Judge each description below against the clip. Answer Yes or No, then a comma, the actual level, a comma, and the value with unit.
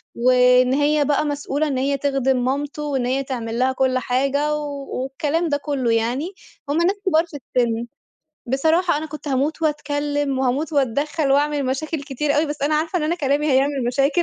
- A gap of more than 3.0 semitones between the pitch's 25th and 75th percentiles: No, narrow, 2.4 semitones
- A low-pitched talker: No, very high, 285 Hz